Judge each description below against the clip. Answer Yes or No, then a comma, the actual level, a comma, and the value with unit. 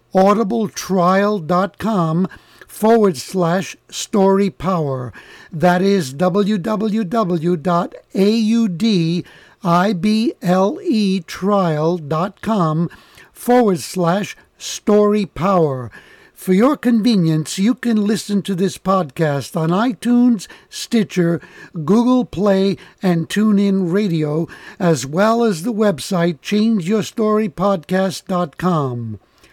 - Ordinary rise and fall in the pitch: Yes, average, 3.7 semitones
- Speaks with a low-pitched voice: No, high, 195 Hz